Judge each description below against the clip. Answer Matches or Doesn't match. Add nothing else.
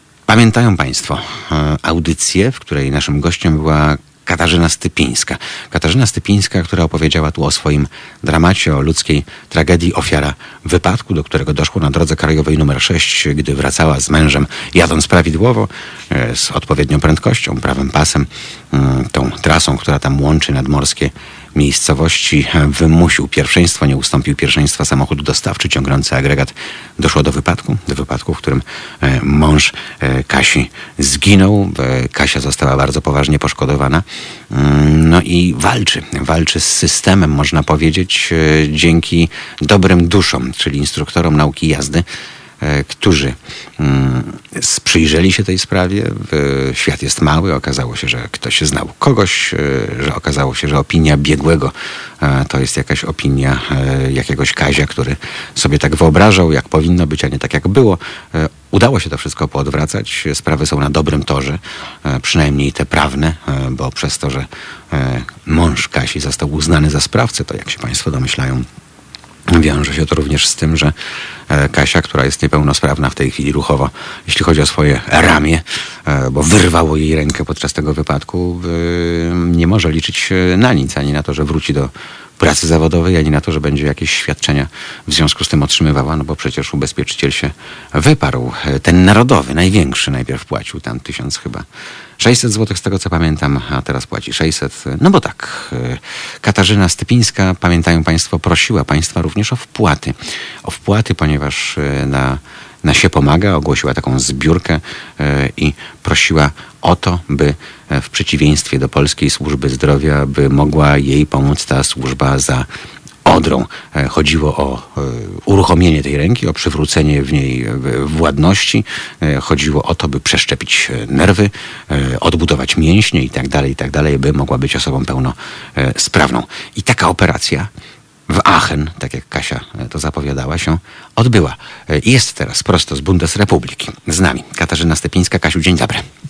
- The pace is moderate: Matches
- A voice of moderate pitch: Doesn't match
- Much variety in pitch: Doesn't match